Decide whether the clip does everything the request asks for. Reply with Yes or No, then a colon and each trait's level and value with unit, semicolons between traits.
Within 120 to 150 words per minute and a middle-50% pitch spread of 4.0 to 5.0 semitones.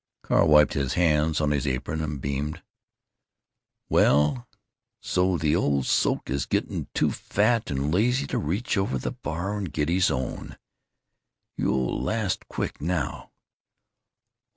Yes: average, 140 wpm; average, 4.6 semitones